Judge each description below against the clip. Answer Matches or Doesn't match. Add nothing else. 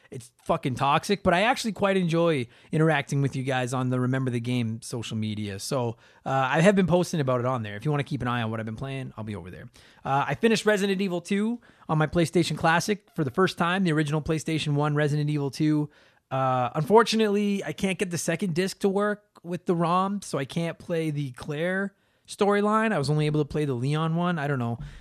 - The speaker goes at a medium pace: Doesn't match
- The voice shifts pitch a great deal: Matches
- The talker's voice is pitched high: Doesn't match